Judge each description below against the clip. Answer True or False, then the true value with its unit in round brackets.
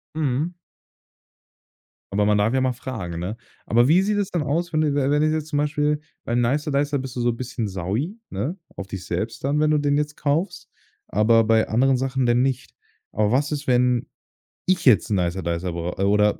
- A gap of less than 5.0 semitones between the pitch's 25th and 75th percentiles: False (5.6 semitones)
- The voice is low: True (130 Hz)